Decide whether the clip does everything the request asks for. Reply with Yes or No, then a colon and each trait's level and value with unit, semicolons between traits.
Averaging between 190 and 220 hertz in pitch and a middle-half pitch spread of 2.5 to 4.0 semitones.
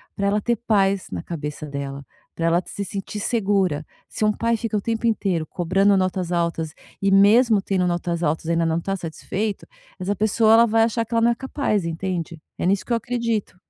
No: high, 195 Hz; average, 4.5 semitones